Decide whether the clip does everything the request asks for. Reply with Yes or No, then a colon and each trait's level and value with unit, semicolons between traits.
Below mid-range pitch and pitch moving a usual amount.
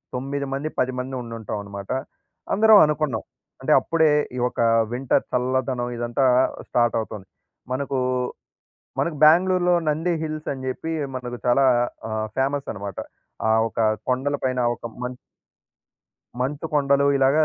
Yes: low, 130 Hz; average, 3.4 semitones